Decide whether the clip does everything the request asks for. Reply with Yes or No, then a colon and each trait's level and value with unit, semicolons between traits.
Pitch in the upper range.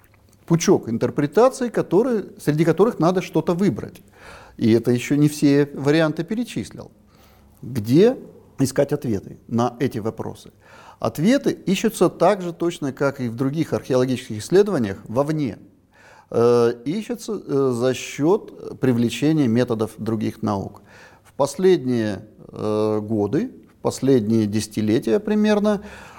No: low, 135 Hz